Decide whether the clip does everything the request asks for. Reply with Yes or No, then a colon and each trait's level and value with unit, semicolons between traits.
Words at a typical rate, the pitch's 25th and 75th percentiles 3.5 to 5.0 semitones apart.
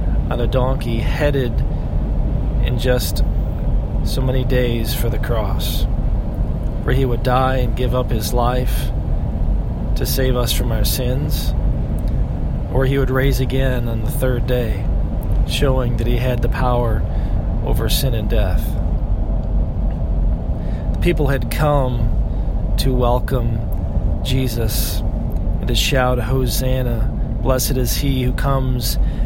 No: slow, 125 wpm; average, 4.4 semitones